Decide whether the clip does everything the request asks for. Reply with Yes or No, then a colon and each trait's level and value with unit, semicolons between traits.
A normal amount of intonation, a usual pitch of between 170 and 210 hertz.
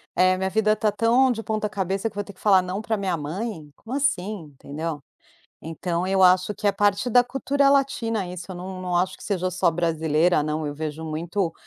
Yes: average, 4.2 semitones; medium, 185 Hz